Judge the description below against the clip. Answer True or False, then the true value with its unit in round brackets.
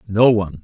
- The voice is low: True (105 Hz)